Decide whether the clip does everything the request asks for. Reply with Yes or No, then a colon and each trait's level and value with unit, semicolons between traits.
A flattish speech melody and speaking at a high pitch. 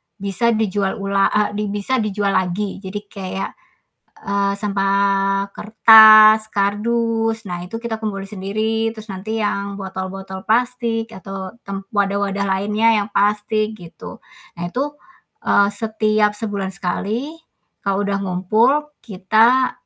Yes: narrow, 2.0 semitones; high, 205 Hz